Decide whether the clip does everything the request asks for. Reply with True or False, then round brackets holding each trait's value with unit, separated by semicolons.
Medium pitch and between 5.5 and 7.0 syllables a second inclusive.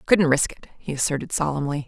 True (150 Hz; 6.0 syllables/s)